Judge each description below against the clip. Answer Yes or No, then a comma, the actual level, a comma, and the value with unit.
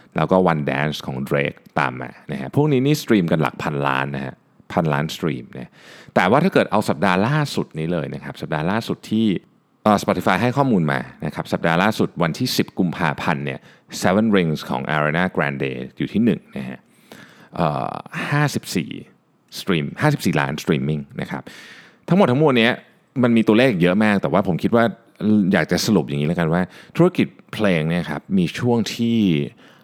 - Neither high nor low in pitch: No, very low, 95 Hz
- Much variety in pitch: Yes, wide, 8.7 semitones